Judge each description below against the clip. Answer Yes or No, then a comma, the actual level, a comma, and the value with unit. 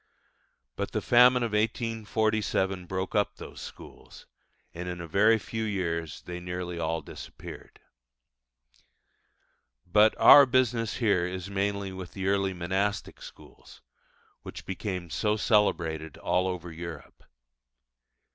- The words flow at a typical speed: No, slow, 120 wpm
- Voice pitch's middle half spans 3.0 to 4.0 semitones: Yes, average, 3.4 semitones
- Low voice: Yes, very low, 95 Hz